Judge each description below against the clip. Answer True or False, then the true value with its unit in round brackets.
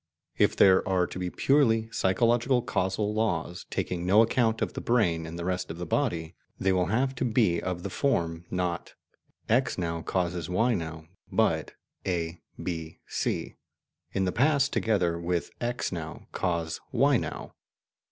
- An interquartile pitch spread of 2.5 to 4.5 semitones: False (5.1 semitones)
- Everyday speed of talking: True (160 wpm)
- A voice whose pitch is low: True (95 Hz)